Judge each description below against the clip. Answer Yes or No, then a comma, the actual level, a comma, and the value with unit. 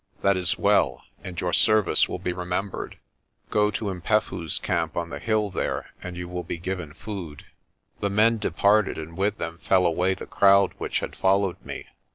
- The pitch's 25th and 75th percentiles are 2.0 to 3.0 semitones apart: Yes, narrow, 2.6 semitones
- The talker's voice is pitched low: Yes, very low, 95 Hz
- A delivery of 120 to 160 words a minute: No, average, 185 wpm